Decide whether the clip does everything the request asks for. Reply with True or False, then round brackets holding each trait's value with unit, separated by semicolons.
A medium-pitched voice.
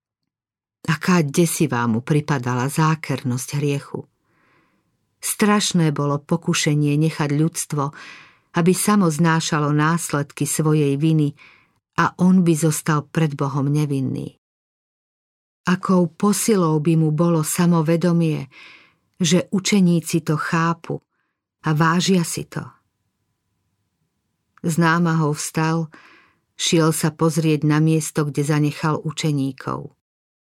True (155 Hz)